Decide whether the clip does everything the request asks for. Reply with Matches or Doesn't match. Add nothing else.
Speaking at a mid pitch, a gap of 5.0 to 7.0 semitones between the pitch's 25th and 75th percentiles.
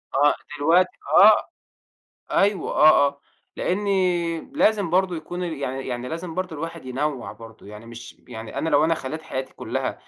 Matches